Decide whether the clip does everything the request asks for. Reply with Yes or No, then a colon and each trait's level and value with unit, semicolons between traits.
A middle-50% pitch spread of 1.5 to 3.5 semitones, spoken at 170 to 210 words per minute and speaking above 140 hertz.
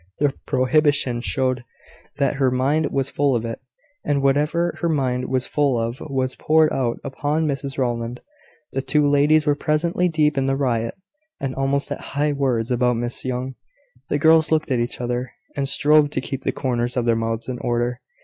No: average, 2.9 semitones; average, 190 wpm; low, 135 Hz